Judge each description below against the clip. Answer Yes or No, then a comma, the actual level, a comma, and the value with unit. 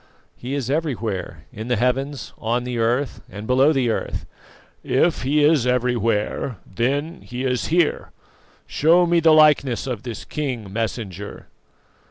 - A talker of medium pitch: No, low, 125 Hz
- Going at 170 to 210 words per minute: No, average, 145 wpm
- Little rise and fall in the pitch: No, average, 4.1 semitones